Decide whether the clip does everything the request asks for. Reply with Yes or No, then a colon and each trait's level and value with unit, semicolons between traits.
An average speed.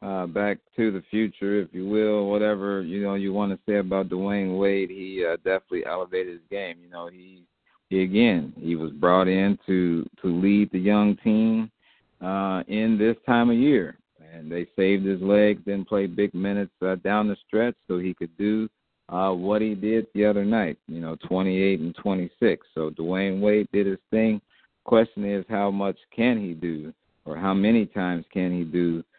Yes: average, 195 wpm